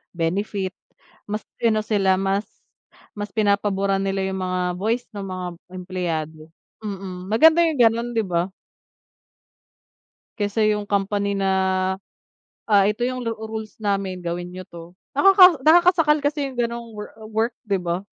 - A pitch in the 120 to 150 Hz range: No, high, 205 Hz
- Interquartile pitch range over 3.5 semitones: No, average, 3.1 semitones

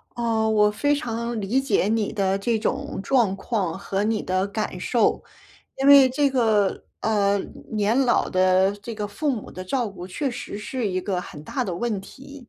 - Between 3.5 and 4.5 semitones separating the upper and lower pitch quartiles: Yes, average, 3.8 semitones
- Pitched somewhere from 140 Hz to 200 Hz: No, high, 215 Hz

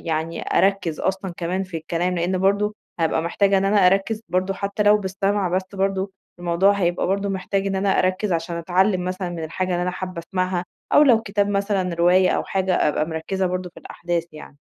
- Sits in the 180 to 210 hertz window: Yes, medium, 185 Hz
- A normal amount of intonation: No, narrow, 2.1 semitones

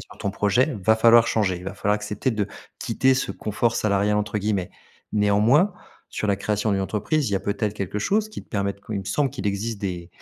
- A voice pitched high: No, low, 105 Hz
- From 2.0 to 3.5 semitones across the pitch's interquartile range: Yes, narrow, 2.6 semitones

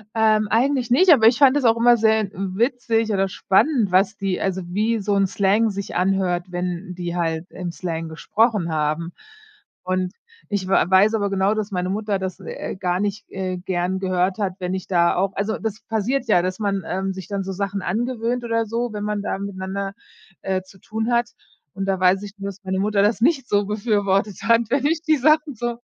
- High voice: Yes, high, 200 Hz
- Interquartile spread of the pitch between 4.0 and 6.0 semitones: No, average, 3.2 semitones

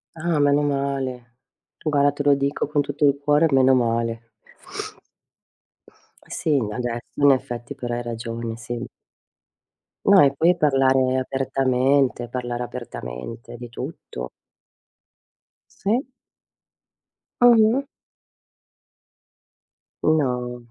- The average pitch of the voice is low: Yes, low, 130 Hz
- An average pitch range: Yes, average, 3.1 semitones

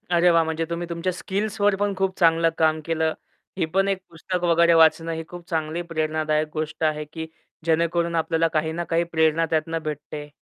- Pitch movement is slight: Yes, narrow, 1.4 semitones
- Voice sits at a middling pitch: Yes, medium, 165 Hz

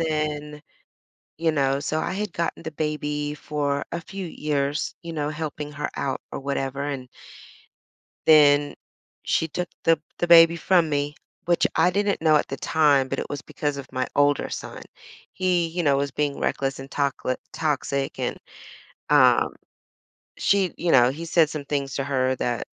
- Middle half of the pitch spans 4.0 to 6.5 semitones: No, average, 2.7 semitones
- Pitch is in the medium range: Yes, medium, 150 Hz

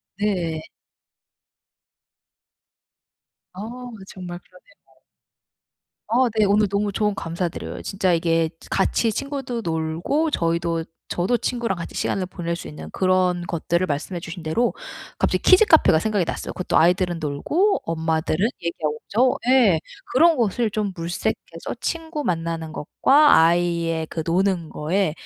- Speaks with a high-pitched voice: No, medium, 180 Hz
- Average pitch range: Yes, average, 5.0 semitones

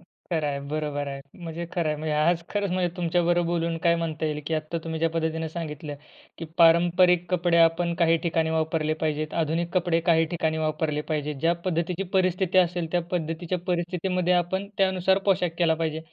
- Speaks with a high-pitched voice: No, medium, 165 Hz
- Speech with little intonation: Yes, narrow, 1.9 semitones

